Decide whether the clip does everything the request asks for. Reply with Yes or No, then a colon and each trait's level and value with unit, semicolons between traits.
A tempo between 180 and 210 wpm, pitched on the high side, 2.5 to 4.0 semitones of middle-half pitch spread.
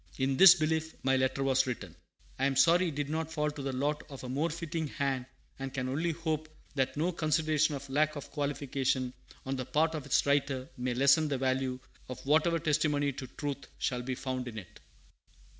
No: fast, 205 wpm; medium, 140 Hz; average, 2.9 semitones